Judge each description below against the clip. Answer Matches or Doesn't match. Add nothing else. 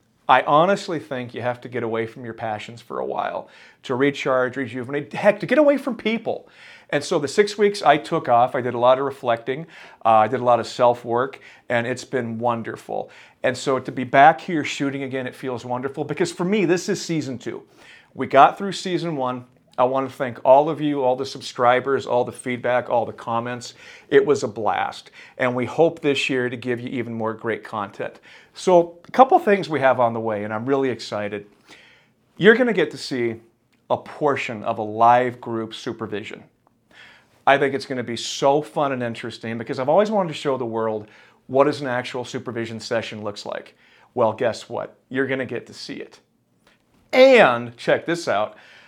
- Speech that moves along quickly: Matches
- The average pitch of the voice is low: Matches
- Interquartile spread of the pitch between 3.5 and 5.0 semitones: Matches